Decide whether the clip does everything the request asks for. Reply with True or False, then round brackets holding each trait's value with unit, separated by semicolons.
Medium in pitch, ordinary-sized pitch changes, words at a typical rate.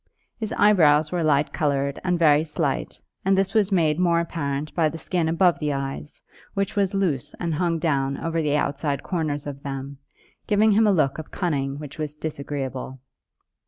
True (155 Hz; 3.9 semitones; 180 wpm)